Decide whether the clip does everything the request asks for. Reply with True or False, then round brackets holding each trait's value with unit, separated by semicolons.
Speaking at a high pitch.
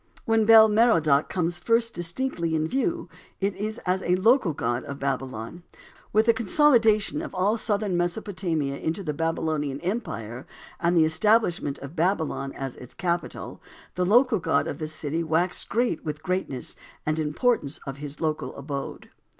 False (175 Hz)